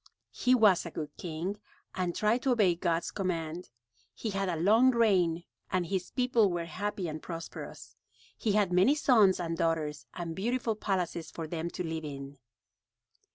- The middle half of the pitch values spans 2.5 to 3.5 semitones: No, average, 4.2 semitones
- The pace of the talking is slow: No, average, 165 wpm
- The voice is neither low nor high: Yes, medium, 180 Hz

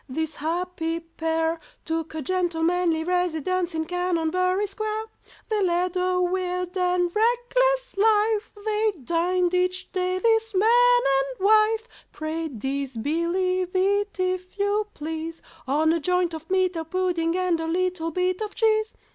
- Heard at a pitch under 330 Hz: No, very high, 360 Hz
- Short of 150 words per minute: Yes, average, 140 wpm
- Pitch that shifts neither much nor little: Yes, average, 3.5 semitones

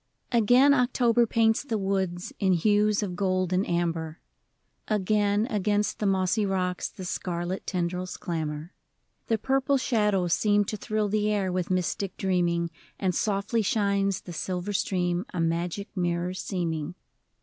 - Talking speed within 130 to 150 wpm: Yes, average, 145 wpm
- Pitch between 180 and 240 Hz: Yes, high, 190 Hz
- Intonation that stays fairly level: No, average, 3.0 semitones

